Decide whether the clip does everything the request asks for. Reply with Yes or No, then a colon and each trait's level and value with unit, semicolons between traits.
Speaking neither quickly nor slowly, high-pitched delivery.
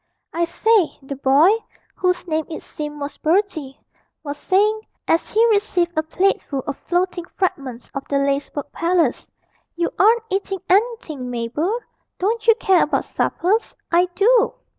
Yes: average, 145 wpm; very high, 345 Hz